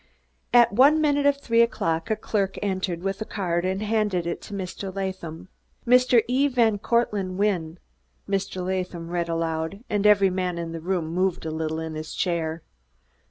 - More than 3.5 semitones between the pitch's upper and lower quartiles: Yes, average, 4.1 semitones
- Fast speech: No, average, 175 wpm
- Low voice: No, high, 190 Hz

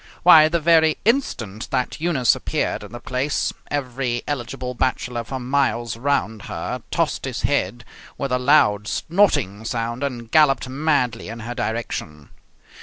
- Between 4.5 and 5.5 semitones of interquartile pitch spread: No, average, 3.8 semitones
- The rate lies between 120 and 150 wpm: Yes, average, 145 wpm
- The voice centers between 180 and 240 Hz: No, low, 125 Hz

